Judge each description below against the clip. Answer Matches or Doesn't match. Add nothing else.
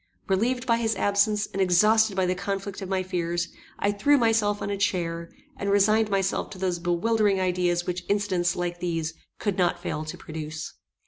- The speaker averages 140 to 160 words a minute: Doesn't match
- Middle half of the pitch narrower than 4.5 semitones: Matches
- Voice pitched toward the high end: Matches